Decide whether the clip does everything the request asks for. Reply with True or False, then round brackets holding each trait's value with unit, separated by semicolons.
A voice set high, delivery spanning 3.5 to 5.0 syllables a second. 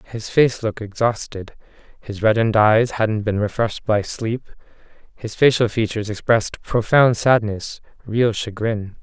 False (110 Hz; 4.6 syllables/s)